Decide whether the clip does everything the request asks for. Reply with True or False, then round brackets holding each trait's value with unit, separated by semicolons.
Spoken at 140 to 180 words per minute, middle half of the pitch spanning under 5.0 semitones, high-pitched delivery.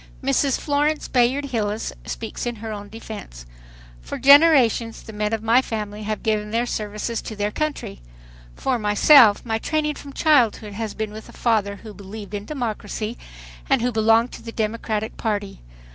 True (170 wpm; 2.9 semitones; 225 Hz)